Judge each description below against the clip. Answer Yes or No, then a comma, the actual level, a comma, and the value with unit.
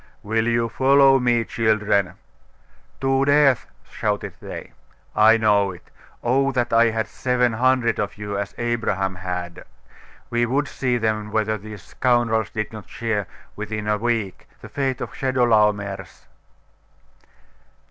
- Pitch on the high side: No, low, 115 Hz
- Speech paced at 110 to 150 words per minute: Yes, slow, 135 wpm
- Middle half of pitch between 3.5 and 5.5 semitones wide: No, average, 2.8 semitones